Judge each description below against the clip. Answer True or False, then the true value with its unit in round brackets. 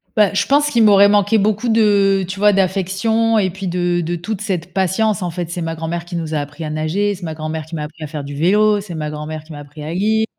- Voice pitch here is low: False (180 Hz)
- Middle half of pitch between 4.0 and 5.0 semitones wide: True (4.3 semitones)